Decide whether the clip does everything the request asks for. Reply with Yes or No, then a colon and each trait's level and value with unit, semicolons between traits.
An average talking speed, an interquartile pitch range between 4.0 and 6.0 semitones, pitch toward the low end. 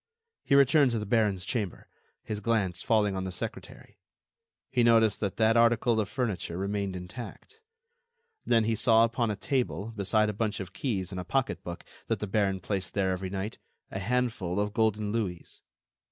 No: average, 175 wpm; average, 3.3 semitones; low, 105 Hz